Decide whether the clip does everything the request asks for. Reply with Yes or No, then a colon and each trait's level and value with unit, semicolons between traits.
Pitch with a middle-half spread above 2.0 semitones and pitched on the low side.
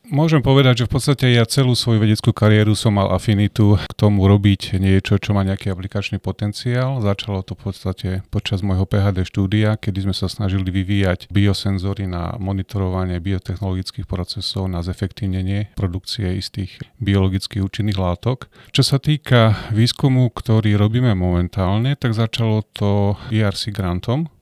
Yes: average, 2.9 semitones; low, 100 Hz